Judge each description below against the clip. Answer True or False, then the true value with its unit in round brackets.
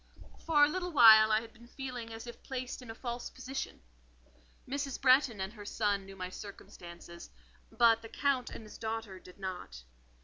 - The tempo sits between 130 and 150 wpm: False (175 wpm)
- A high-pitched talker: True (225 Hz)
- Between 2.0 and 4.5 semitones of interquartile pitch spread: True (4.2 semitones)